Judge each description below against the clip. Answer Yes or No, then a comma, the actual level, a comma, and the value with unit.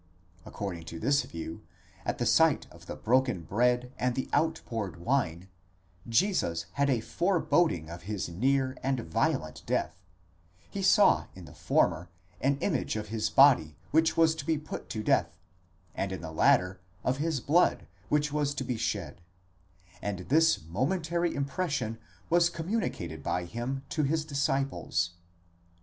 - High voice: No, low, 130 Hz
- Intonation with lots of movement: Yes, wide, 8.6 semitones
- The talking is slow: No, average, 155 wpm